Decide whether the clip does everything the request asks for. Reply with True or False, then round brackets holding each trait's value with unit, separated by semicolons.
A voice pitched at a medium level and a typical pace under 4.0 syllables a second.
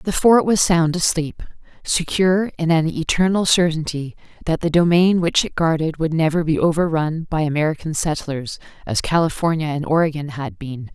False (160 Hz; 5.0 syllables/s)